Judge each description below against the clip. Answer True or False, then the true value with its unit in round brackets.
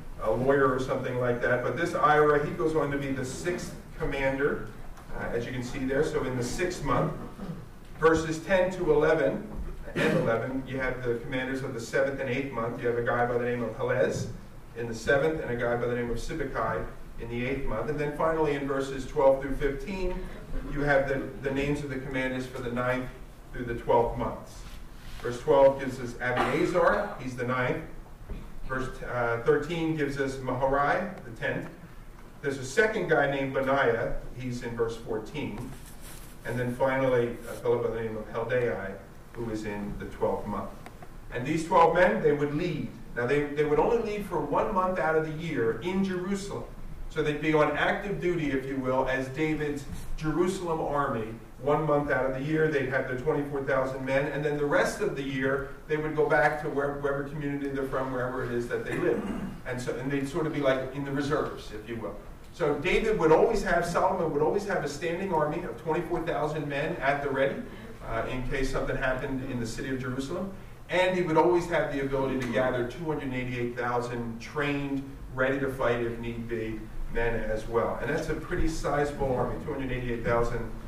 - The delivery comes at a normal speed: False (210 wpm)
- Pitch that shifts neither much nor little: True (3.6 semitones)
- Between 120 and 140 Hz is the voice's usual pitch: True (135 Hz)